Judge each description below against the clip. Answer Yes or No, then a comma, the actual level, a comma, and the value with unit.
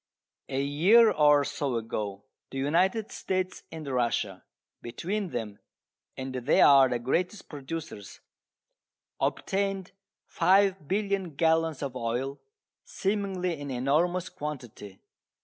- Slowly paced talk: Yes, slow, 105 wpm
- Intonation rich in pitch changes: Yes, wide, 6.2 semitones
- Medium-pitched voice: Yes, medium, 150 Hz